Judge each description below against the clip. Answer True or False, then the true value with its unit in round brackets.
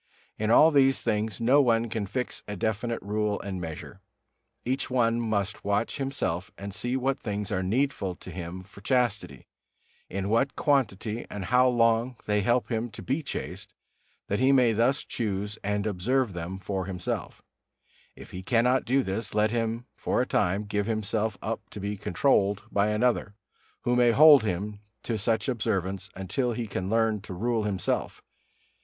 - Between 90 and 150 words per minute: False (170 wpm)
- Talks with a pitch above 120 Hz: False (110 Hz)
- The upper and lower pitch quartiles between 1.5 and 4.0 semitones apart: True (3.4 semitones)